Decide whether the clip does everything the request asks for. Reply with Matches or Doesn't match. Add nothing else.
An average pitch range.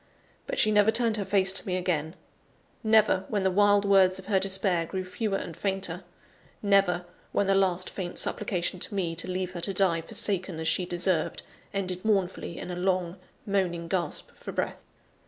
Doesn't match